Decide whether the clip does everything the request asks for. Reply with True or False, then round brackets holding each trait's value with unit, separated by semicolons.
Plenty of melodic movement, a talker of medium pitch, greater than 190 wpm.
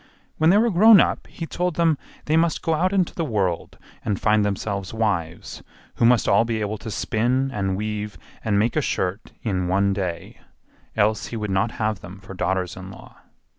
False (5.8 semitones; 110 Hz; 200 wpm)